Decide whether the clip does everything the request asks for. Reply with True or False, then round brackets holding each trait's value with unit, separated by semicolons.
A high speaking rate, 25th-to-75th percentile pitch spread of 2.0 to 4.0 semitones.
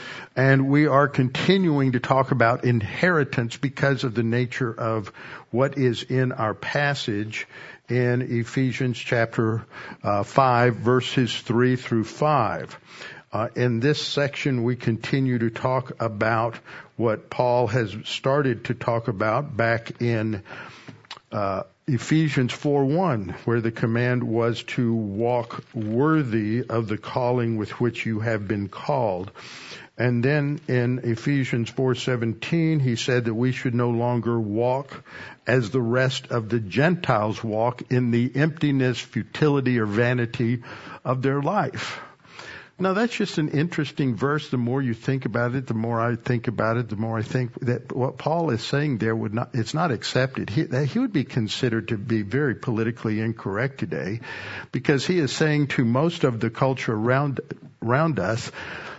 False (155 wpm; 3.1 semitones)